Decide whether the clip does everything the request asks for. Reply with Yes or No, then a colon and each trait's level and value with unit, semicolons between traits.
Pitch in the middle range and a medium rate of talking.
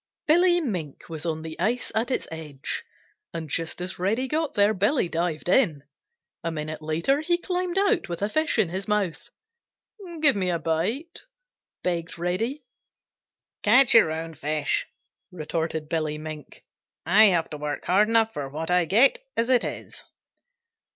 Yes: medium, 180 Hz; average, 160 wpm